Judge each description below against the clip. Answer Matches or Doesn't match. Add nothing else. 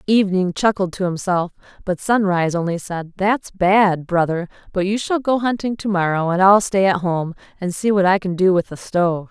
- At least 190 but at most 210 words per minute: Matches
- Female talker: Matches